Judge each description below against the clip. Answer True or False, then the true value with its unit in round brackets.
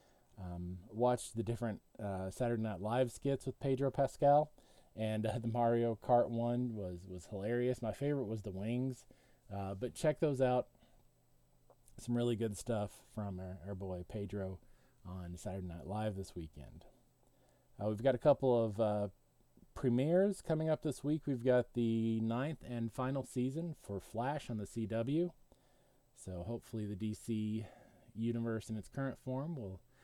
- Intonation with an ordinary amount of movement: True (4.0 semitones)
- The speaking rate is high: False (160 wpm)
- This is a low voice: True (115 Hz)